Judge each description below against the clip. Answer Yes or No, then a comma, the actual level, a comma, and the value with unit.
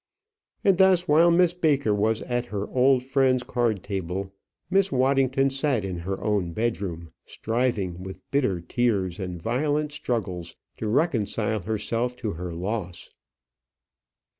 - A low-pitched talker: Yes, low, 115 Hz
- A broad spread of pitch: Yes, wide, 5.9 semitones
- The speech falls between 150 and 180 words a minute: No, slow, 135 wpm